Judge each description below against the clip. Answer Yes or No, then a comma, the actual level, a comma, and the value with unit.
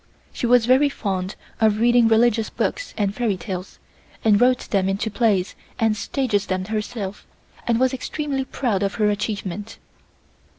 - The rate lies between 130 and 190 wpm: Yes, average, 155 wpm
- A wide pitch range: No, average, 3.3 semitones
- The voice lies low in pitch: No, high, 220 Hz